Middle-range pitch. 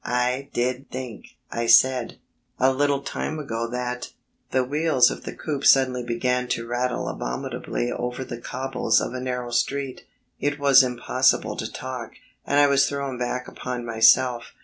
No: low, 125 Hz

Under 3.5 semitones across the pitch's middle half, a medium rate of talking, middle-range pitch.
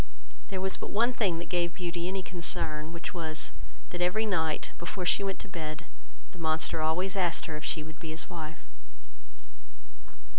Yes: average, 2.8 semitones; average, 180 wpm; medium, 170 Hz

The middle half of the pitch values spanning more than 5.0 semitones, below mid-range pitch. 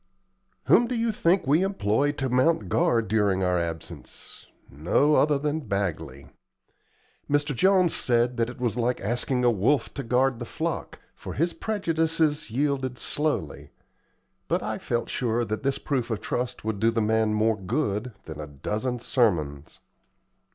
Yes: wide, 5.5 semitones; low, 125 Hz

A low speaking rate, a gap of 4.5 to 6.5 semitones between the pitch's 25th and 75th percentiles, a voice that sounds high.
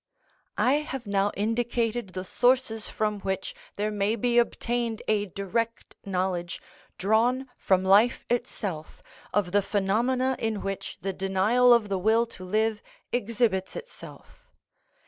No: slow, 130 wpm; average, 3.5 semitones; high, 215 Hz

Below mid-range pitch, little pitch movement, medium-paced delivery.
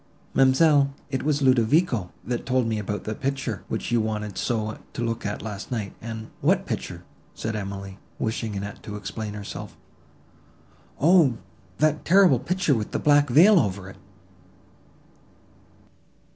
No: low, 115 Hz; average, 4.8 semitones; average, 145 wpm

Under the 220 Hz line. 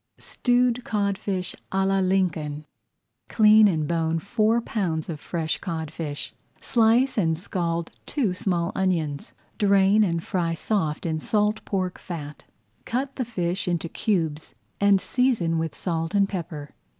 Yes: medium, 185 Hz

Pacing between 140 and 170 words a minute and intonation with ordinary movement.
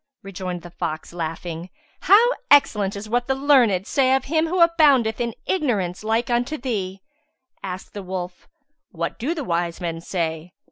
No: average, 160 wpm; wide, 7.1 semitones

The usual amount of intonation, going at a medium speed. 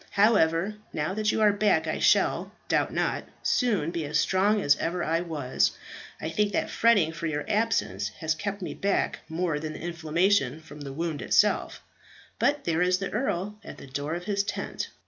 Yes: average, 4.5 semitones; average, 190 wpm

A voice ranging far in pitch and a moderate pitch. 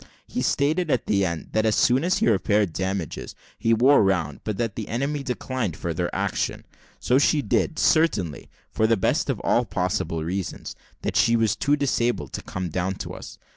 No: wide, 5.9 semitones; low, 110 Hz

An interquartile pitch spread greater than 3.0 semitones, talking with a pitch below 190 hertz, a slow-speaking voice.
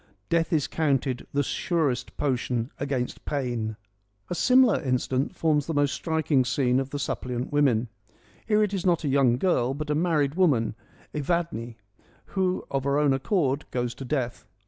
No: average, 4.1 semitones; medium, 140 Hz; average, 165 wpm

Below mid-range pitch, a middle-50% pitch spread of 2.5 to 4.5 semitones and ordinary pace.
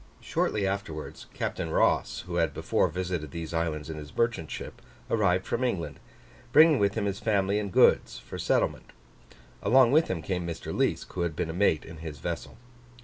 Yes: very low, 90 Hz; average, 4.0 semitones; average, 185 wpm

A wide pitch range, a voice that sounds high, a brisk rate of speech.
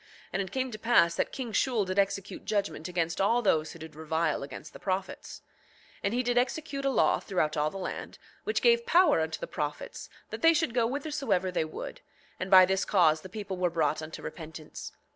Yes: wide, 7.0 semitones; high, 195 Hz; fast, 215 wpm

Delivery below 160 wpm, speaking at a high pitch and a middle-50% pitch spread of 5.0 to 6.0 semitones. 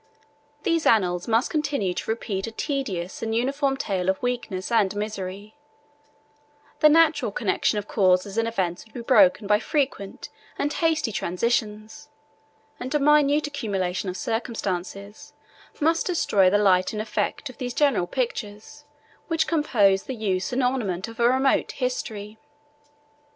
Yes: average, 145 wpm; high, 225 Hz; wide, 5.5 semitones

